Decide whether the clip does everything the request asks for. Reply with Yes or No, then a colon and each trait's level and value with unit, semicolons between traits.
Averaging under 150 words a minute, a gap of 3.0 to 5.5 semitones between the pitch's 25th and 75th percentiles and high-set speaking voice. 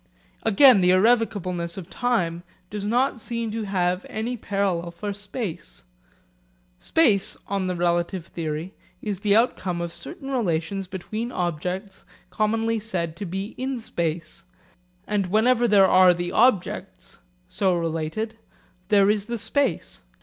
Yes: slow, 135 wpm; average, 4.2 semitones; high, 195 Hz